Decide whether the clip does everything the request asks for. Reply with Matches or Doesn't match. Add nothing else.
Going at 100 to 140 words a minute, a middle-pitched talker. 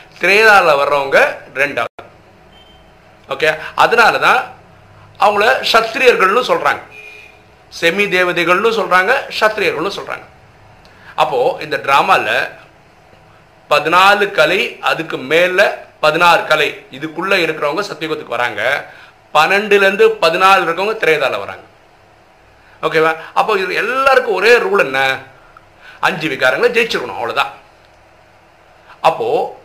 Doesn't match